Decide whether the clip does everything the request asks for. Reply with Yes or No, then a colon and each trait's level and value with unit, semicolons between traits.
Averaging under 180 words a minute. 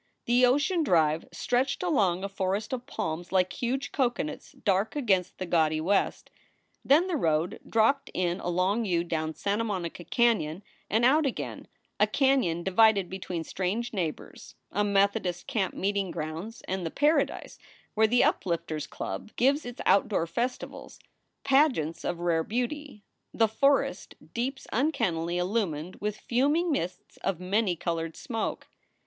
Yes: average, 145 wpm